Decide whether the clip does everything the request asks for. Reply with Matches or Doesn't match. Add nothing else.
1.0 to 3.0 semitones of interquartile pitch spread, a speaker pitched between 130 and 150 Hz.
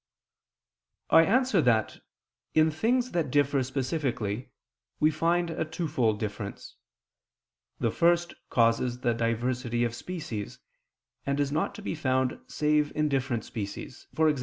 Doesn't match